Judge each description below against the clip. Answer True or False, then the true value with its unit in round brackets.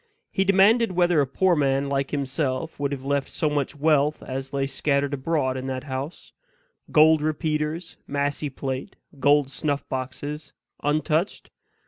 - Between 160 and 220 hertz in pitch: False (145 Hz)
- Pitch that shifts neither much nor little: False (2.3 semitones)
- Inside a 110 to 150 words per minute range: True (145 wpm)